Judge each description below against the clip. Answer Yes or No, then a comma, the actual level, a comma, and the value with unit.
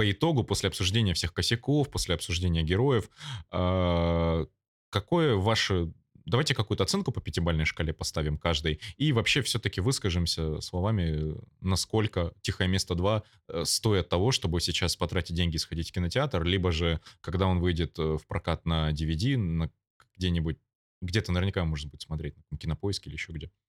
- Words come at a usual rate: Yes, average, 150 wpm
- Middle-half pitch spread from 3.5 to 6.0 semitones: Yes, average, 3.9 semitones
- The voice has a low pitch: Yes, very low, 90 Hz